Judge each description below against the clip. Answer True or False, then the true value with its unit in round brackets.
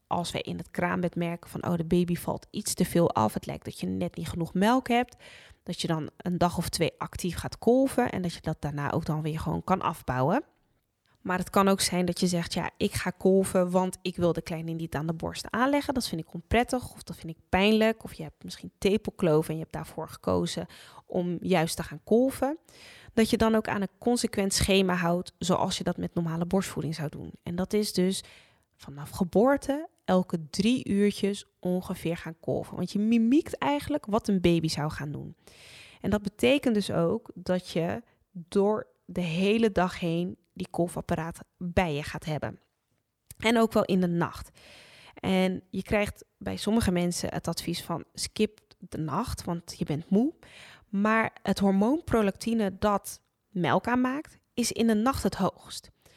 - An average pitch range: True (4.2 semitones)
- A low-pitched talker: False (185 Hz)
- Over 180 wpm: True (195 wpm)